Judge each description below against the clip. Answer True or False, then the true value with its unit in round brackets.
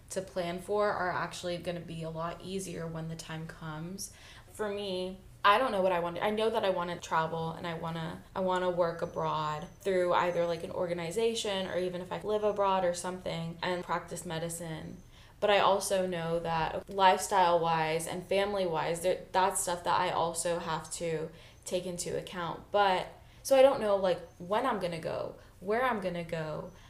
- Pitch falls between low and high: True (175 Hz)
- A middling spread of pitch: False (2.3 semitones)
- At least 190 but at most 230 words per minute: True (200 wpm)